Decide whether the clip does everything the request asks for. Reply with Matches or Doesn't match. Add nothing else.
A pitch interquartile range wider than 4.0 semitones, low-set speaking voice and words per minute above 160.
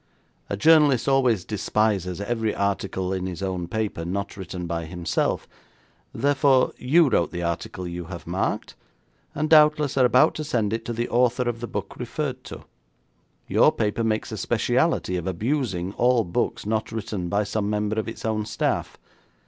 Matches